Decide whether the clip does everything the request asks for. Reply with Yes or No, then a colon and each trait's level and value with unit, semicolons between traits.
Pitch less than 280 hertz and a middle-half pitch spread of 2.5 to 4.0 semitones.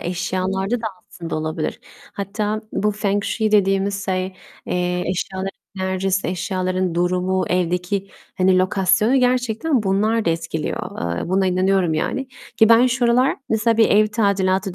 Yes: high, 190 Hz; average, 2.8 semitones